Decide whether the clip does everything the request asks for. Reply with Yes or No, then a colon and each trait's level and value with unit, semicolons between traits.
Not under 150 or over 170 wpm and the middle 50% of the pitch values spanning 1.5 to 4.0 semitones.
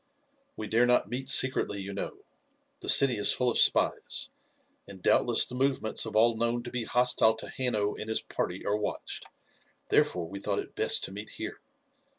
No: average, 185 wpm; average, 3.1 semitones